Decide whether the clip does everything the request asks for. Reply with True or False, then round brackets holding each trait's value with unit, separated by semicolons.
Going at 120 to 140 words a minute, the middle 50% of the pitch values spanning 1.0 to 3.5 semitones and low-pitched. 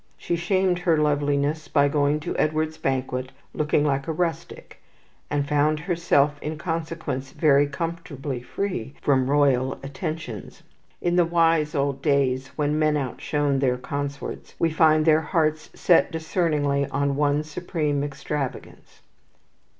False (135 wpm; 2.4 semitones; 150 Hz)